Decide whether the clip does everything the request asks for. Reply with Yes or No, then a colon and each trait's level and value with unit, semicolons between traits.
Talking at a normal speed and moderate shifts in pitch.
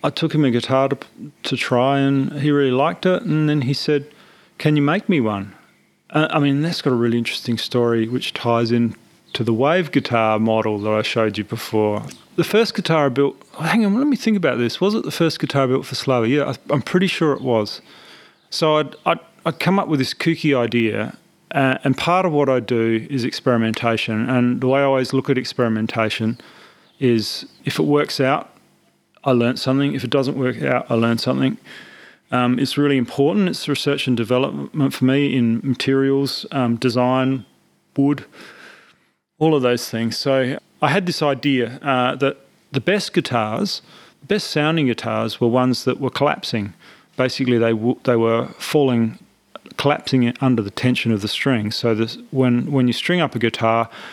Yes: average, 195 wpm; average, 3.7 semitones